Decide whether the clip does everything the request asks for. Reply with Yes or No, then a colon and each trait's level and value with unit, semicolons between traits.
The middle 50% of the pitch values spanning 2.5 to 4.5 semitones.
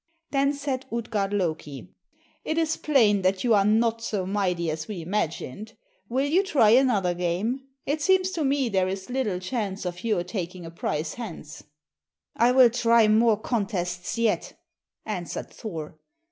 No: wide, 5.5 semitones